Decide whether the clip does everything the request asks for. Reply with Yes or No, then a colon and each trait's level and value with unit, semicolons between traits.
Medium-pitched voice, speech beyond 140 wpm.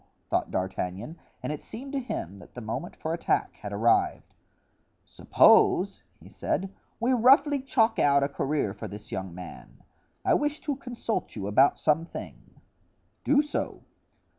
Yes: medium, 155 Hz; average, 155 wpm